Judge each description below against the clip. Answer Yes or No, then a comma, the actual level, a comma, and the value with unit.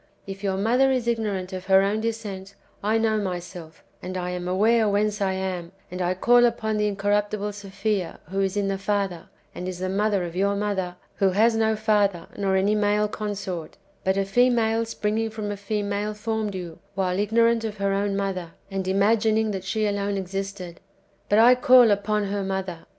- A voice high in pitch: Yes, high, 200 Hz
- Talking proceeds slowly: No, average, 190 wpm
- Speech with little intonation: Yes, narrow, 2.1 semitones